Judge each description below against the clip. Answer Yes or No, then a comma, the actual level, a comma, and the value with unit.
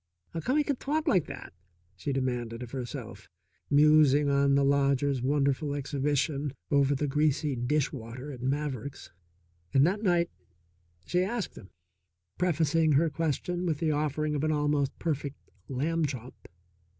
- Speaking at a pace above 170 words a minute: No, average, 150 wpm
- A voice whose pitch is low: No, medium, 145 Hz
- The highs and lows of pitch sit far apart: No, narrow, 2.5 semitones